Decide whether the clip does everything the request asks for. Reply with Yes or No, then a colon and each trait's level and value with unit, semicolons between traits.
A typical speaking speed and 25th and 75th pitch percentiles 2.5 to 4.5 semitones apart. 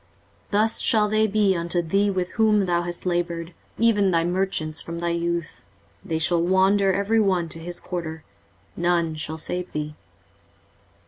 Yes: average, 165 wpm; average, 2.8 semitones